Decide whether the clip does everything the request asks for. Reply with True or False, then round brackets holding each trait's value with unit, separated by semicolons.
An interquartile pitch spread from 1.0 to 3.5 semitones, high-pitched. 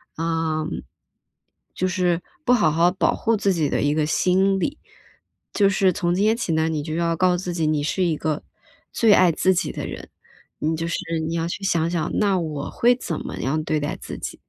False (3.0 semitones; 170 Hz)